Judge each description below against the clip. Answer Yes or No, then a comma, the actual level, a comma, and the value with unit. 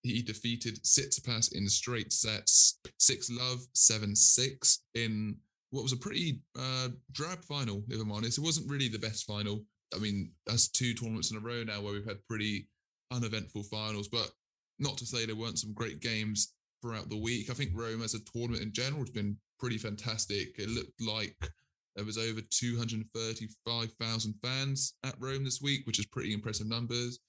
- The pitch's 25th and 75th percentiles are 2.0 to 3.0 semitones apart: Yes, narrow, 2.4 semitones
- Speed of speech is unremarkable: Yes, average, 185 wpm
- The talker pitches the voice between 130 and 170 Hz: No, low, 115 Hz